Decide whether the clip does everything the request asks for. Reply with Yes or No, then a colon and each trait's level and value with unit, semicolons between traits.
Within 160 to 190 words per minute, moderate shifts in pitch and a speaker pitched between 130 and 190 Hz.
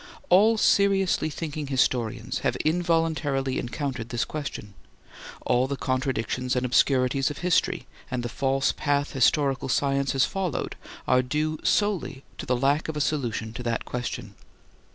No: average, 145 wpm; average, 3.5 semitones; low, 135 Hz